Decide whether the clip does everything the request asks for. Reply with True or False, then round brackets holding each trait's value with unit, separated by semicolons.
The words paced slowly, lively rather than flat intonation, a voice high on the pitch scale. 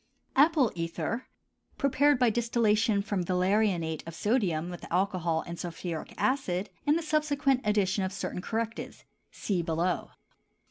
True (130 wpm; 5.8 semitones; 200 Hz)